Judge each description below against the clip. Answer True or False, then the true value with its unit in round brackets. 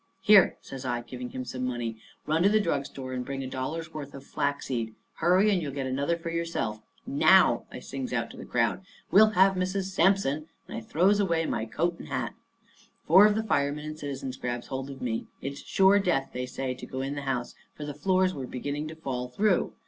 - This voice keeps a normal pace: False (225 wpm)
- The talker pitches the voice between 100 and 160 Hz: True (140 Hz)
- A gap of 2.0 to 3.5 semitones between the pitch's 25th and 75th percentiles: False (5.4 semitones)